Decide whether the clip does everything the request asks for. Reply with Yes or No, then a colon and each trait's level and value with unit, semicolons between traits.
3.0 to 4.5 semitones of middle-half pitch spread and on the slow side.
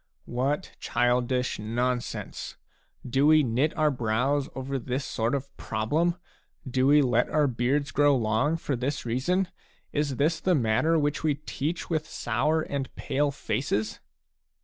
No: average, 3.3 semitones; average, 150 wpm